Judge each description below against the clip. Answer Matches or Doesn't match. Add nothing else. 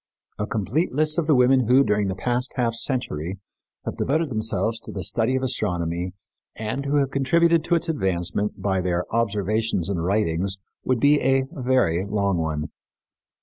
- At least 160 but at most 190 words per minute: Matches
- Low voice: Matches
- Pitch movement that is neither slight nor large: Doesn't match